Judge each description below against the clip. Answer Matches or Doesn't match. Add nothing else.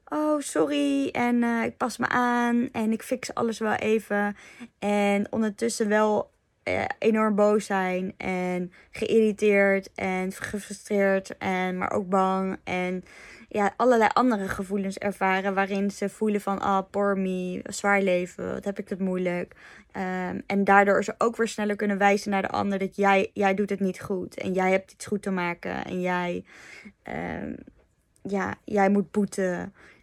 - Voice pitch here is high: Matches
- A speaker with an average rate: Matches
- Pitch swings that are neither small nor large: Doesn't match